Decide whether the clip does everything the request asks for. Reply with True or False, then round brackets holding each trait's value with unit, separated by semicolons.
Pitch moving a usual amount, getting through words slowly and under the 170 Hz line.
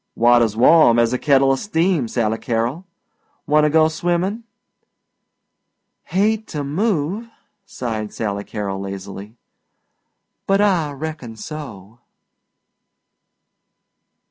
False (7.0 semitones; 90 wpm; 140 Hz)